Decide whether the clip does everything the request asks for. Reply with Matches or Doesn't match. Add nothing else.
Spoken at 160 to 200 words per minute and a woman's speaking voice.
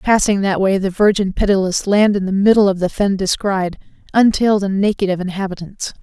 Matches